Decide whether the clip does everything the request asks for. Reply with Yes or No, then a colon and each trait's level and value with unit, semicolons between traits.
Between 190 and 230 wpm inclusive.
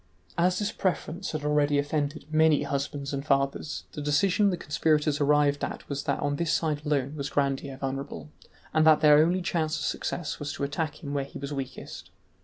Yes: average, 195 wpm